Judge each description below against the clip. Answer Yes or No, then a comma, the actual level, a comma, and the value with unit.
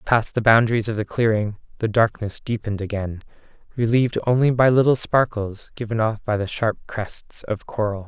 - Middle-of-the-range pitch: No, low, 110 Hz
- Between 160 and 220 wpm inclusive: Yes, average, 170 wpm